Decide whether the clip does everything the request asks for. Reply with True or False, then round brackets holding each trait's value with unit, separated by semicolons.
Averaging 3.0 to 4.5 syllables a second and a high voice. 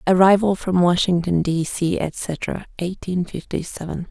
False (4.1 syllables/s; 175 Hz)